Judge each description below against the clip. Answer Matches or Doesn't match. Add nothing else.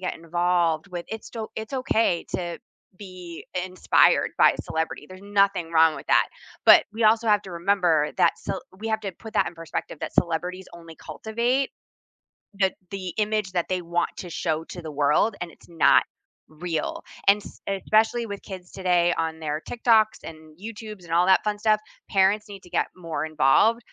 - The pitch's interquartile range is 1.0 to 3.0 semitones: Doesn't match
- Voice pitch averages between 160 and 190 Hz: Matches